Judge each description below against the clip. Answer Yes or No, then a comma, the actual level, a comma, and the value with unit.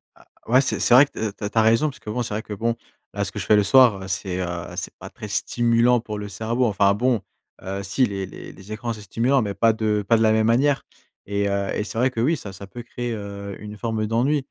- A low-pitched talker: Yes, low, 110 Hz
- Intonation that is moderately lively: Yes, average, 3.1 semitones